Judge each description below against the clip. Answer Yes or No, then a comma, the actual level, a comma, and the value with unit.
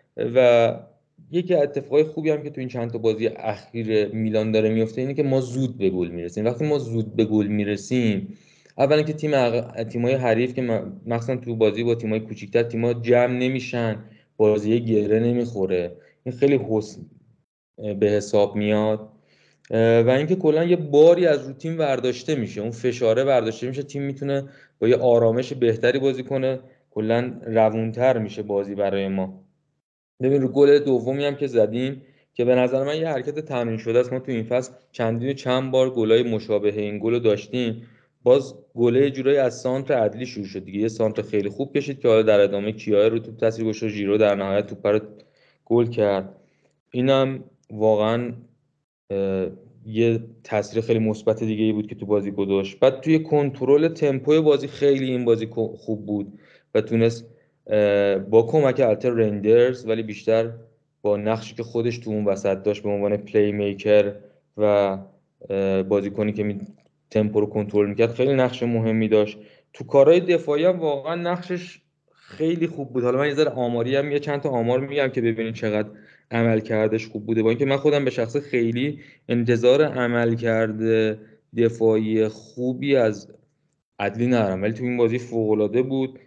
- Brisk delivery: Yes, fast, 165 wpm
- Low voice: Yes, low, 115 Hz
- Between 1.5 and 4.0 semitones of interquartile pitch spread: Yes, average, 3.7 semitones